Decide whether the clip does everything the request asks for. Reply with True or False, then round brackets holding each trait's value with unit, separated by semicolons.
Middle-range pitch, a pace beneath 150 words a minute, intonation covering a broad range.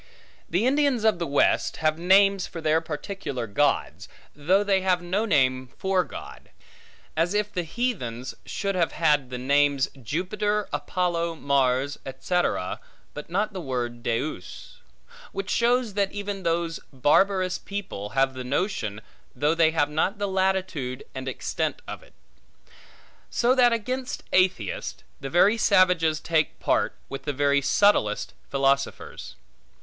True (170 Hz; 140 wpm; 6.2 semitones)